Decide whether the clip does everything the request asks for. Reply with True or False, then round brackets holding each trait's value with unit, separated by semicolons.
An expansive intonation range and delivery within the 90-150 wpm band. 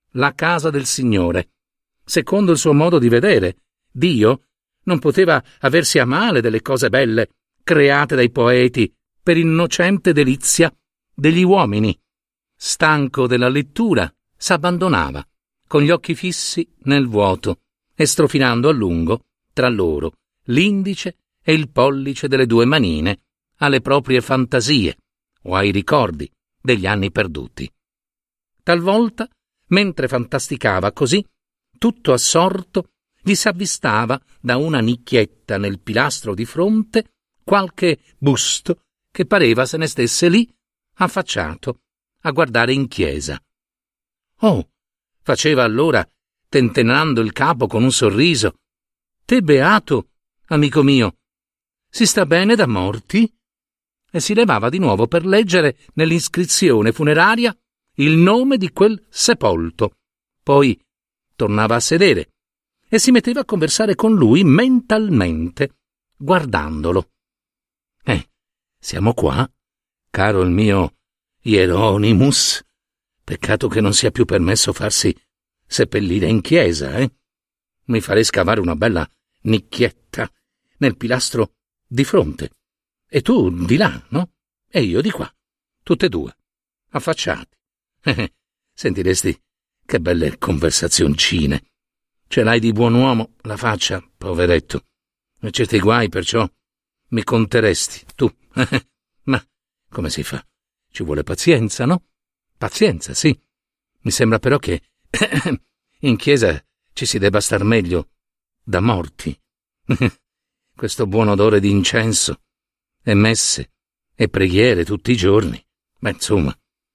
True (7.6 semitones; 120 wpm)